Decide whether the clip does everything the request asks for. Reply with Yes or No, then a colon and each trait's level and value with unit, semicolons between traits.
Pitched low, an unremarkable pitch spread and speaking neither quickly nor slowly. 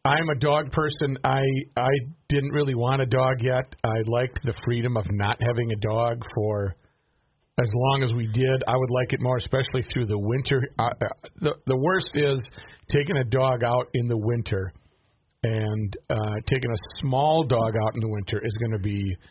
Yes: low, 125 Hz; average, 3.3 semitones; average, 190 wpm